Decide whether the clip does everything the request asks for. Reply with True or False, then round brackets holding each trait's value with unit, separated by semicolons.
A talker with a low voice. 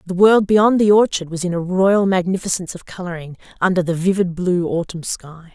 False (180 Hz)